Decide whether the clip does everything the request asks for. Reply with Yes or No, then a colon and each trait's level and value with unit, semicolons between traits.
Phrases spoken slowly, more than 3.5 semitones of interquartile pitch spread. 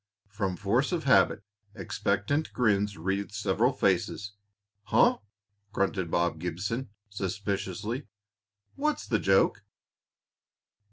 No: slow, 95 wpm; average, 3.0 semitones